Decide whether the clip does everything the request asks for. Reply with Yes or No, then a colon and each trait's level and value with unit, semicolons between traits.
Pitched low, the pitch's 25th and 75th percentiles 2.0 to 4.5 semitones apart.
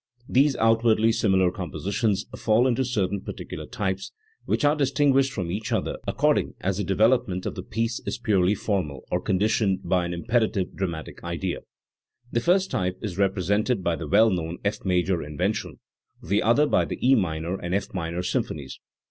Yes: low, 100 Hz; average, 4.0 semitones